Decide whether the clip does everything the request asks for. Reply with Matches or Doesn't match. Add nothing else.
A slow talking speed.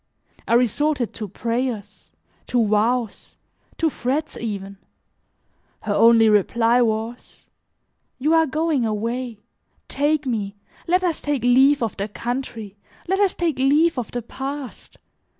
Matches